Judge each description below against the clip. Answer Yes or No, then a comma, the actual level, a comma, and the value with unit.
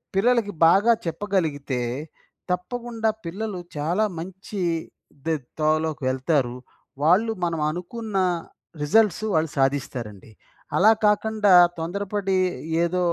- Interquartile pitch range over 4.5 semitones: Yes, average, 5.0 semitones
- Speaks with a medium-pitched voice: Yes, medium, 180 Hz